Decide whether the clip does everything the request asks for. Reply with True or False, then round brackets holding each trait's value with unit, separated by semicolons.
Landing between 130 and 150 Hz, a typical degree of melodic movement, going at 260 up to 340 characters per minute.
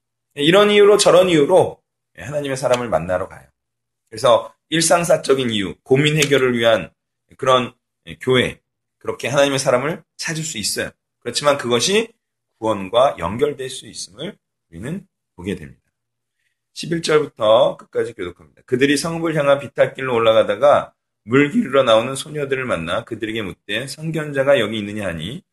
True (135 Hz; 4.8 semitones; 335 characters per minute)